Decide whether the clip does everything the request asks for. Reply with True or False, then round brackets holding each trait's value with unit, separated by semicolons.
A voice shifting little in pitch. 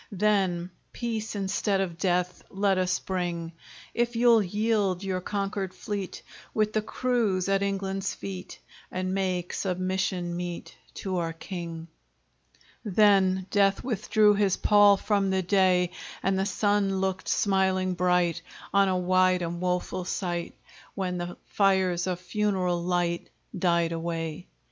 True (1.9 semitones)